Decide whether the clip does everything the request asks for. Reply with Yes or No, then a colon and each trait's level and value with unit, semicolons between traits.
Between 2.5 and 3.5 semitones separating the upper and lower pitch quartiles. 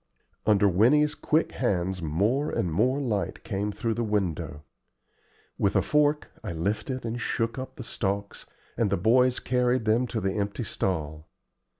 No: average, 4.5 semitones